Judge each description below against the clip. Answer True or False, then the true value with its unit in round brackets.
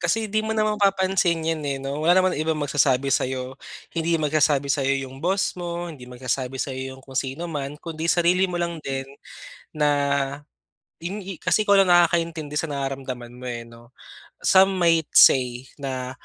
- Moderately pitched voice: True (150 Hz)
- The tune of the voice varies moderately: True (4.6 semitones)